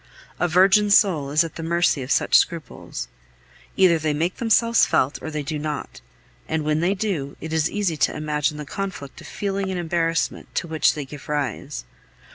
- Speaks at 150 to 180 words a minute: No, average, 190 wpm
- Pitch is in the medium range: Yes, medium, 160 Hz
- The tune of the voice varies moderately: Yes, average, 3.7 semitones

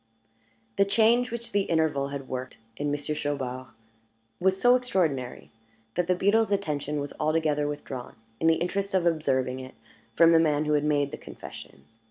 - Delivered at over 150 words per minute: Yes, average, 170 wpm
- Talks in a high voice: No, medium, 155 Hz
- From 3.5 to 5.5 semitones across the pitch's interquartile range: Yes, average, 5.1 semitones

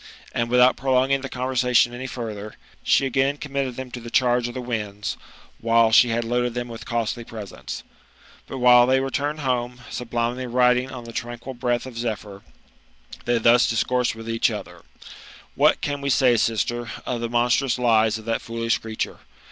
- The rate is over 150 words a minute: Yes, average, 175 wpm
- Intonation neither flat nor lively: No, narrow, 1.7 semitones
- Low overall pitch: Yes, low, 120 Hz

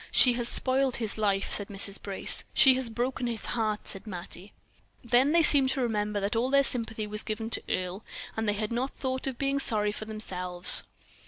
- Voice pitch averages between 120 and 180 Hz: No, high, 225 Hz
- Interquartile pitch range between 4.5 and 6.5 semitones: No, average, 3.7 semitones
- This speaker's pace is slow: No, average, 200 wpm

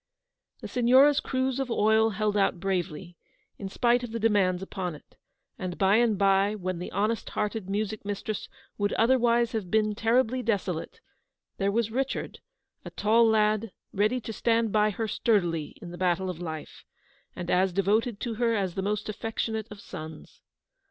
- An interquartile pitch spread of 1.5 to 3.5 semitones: Yes, average, 3.0 semitones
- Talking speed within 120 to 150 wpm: No, average, 170 wpm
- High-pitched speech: Yes, high, 210 Hz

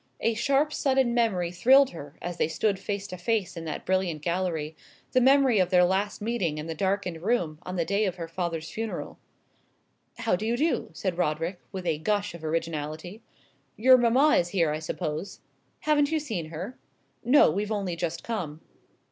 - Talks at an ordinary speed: Yes, average, 185 wpm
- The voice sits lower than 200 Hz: Yes, medium, 185 Hz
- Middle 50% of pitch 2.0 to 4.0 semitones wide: No, wide, 5.5 semitones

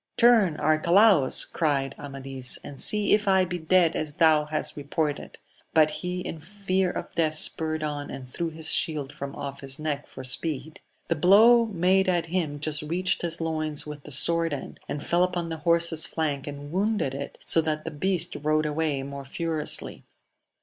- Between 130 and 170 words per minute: No, average, 185 wpm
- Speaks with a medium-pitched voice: Yes, medium, 155 Hz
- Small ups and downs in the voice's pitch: No, average, 3.3 semitones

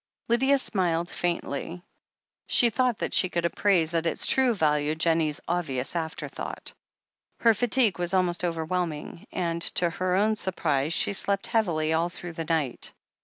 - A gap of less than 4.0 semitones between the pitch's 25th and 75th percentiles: Yes, average, 3.5 semitones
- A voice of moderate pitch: Yes, medium, 175 Hz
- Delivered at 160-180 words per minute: No, average, 150 wpm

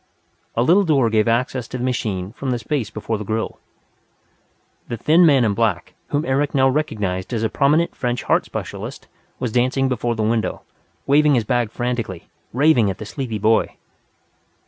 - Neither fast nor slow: Yes, average, 175 wpm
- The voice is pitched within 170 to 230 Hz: No, low, 120 Hz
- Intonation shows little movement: No, average, 3.7 semitones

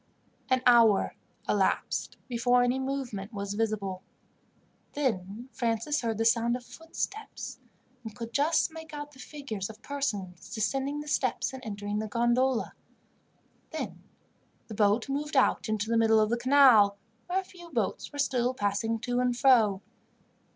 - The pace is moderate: Yes, average, 150 wpm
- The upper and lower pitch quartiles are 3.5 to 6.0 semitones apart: Yes, average, 4.1 semitones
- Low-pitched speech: No, high, 240 Hz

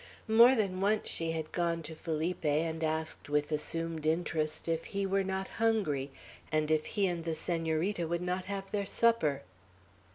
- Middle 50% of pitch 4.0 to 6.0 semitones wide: No, average, 3.6 semitones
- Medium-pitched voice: Yes, medium, 165 Hz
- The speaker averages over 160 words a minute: Yes, average, 170 wpm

